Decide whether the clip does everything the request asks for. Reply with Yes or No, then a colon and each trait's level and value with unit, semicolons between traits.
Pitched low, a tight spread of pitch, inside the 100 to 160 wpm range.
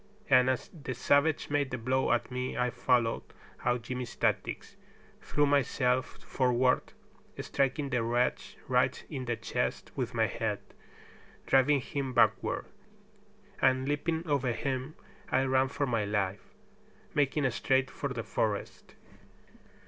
Yes: low, 130 Hz; narrow, 2.2 semitones; slow, 135 wpm